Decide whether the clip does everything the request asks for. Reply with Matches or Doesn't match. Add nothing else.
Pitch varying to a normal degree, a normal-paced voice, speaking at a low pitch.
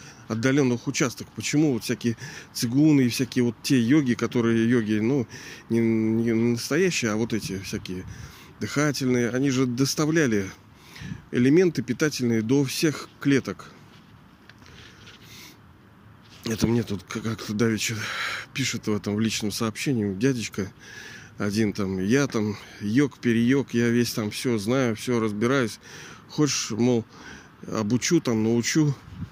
Matches